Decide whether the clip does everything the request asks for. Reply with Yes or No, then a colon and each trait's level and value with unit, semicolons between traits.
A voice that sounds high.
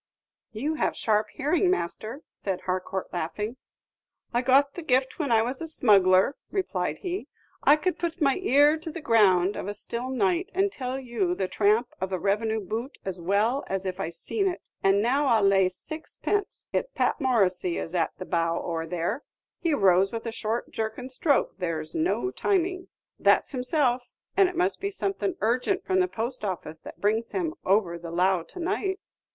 Yes: high, 235 Hz